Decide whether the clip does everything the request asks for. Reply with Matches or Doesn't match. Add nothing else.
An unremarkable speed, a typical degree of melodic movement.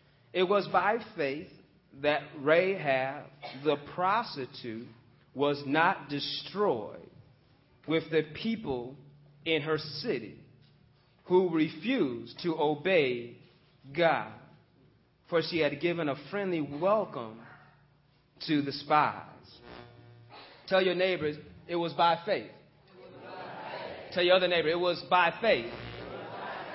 Doesn't match